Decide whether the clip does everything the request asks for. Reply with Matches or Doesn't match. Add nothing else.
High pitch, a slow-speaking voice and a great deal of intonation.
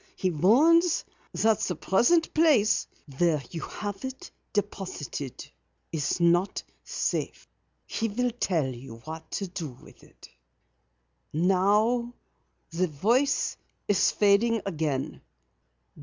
Matches